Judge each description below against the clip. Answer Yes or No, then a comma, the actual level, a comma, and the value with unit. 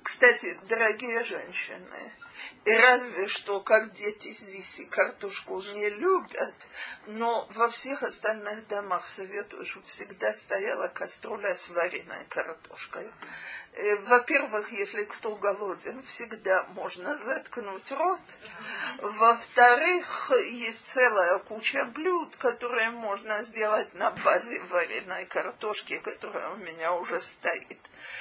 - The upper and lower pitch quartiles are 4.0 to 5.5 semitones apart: No, average, 3.3 semitones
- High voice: Yes, high, 220 Hz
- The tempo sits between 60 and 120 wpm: Yes, slow, 110 wpm